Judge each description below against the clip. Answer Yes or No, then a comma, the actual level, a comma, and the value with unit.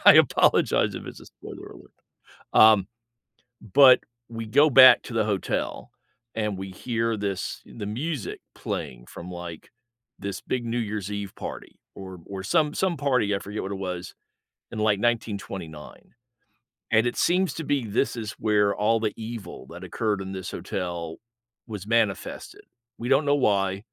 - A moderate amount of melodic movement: Yes, average, 3.6 semitones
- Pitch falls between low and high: No, low, 105 Hz